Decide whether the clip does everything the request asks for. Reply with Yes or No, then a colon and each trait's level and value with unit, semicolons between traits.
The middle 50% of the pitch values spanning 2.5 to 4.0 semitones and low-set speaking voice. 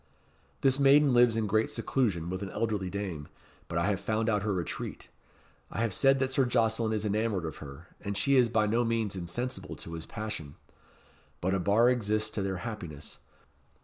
Yes: average, 3.6 semitones; low, 110 Hz